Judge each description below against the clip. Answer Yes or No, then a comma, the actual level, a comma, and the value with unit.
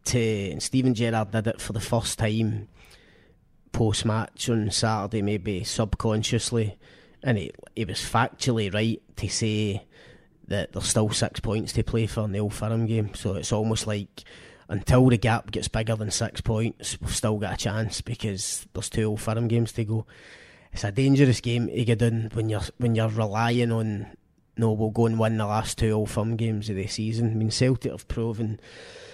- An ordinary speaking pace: Yes, average, 190 wpm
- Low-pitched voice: Yes, low, 110 Hz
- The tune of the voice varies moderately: No, narrow, 1.5 semitones